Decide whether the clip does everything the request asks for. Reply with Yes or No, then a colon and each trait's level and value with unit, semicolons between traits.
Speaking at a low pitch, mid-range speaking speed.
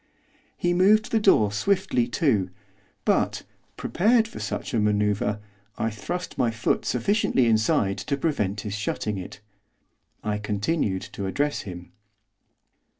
No: low, 110 Hz; slow, 130 wpm